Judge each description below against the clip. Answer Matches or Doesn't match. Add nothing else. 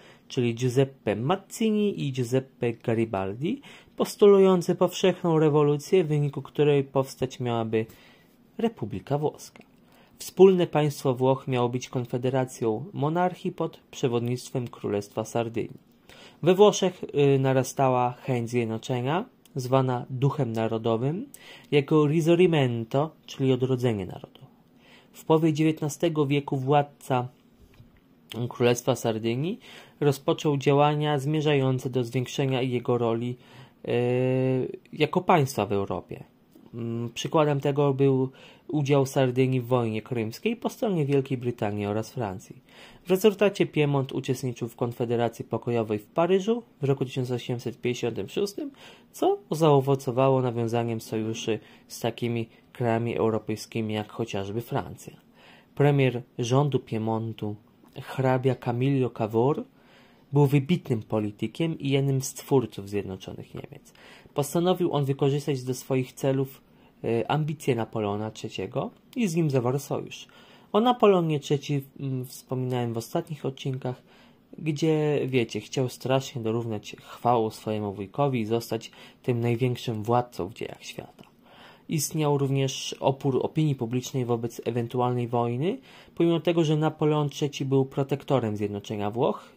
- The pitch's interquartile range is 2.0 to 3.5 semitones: Doesn't match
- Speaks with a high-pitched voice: Doesn't match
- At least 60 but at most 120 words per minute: Matches